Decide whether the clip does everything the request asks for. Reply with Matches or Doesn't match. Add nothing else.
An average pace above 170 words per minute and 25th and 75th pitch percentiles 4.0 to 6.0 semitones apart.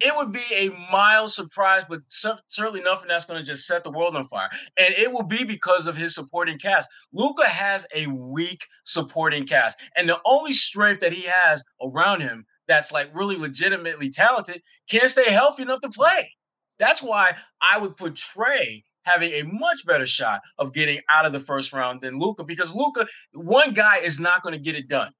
Matches